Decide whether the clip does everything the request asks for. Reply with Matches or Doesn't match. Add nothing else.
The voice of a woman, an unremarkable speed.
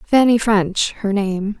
Matches